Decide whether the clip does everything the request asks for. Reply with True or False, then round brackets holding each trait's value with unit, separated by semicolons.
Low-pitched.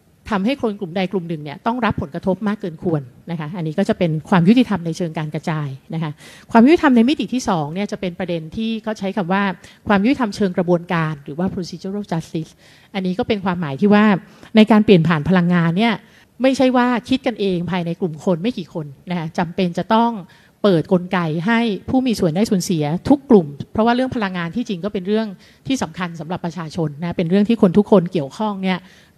False (190 Hz)